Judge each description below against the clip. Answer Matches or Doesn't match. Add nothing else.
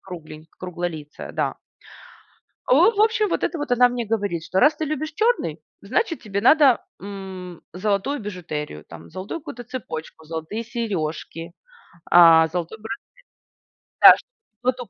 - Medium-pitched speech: Doesn't match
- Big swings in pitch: Matches